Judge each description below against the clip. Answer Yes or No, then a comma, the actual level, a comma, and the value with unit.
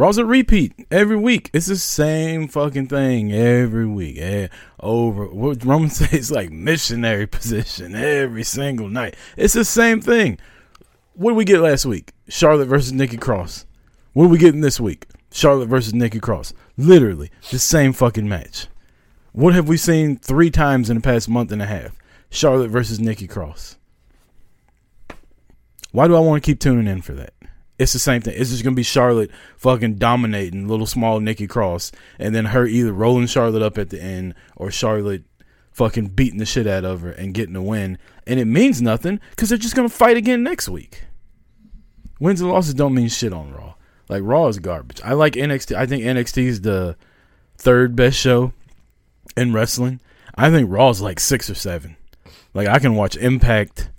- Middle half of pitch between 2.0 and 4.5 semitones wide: No, wide, 5.5 semitones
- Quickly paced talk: No, average, 185 wpm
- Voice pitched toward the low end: Yes, low, 120 Hz